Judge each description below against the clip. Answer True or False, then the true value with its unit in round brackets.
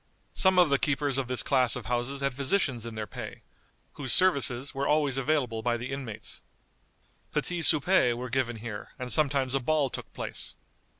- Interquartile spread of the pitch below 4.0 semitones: True (3.1 semitones)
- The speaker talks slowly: False (180 wpm)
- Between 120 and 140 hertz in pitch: True (135 Hz)